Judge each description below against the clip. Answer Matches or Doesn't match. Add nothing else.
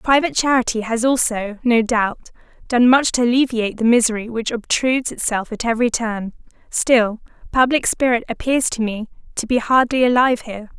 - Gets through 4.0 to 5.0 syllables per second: Doesn't match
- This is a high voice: Matches